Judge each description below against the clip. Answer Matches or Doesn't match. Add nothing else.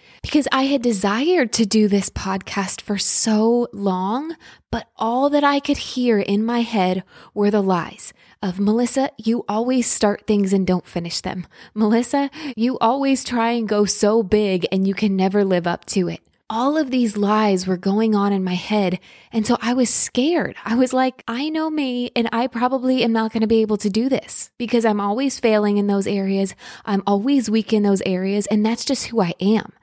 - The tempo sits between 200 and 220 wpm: Matches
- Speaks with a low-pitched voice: Doesn't match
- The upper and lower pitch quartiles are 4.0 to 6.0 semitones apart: Doesn't match